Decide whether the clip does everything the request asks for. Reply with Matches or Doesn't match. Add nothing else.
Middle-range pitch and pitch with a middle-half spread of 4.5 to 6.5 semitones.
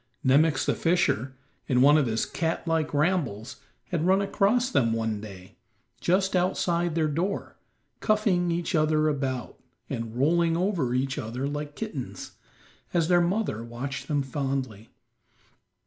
Matches